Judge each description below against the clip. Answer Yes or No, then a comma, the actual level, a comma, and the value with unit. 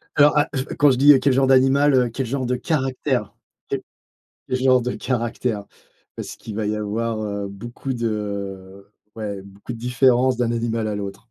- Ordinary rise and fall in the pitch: Yes, average, 3.7 semitones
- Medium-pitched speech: No, low, 120 Hz